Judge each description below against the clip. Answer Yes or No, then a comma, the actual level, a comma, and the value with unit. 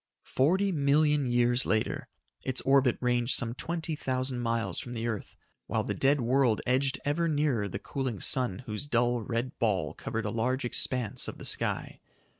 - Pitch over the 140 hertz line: No, low, 125 Hz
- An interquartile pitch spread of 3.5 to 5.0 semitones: No, average, 3.1 semitones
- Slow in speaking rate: No, average, 170 wpm